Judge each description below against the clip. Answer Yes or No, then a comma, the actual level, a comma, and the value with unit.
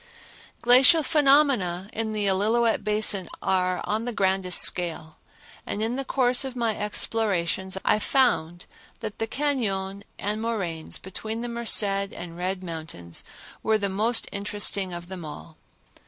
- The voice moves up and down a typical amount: Yes, average, 4.0 semitones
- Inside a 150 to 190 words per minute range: No, average, 140 wpm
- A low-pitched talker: No, high, 205 Hz